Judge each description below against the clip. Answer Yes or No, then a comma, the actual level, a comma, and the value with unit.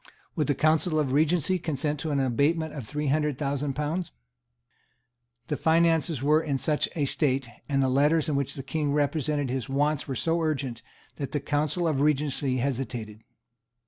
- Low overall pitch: No, medium, 145 Hz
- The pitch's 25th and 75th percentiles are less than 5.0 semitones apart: Yes, narrow, 2.4 semitones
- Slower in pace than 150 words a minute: No, average, 175 wpm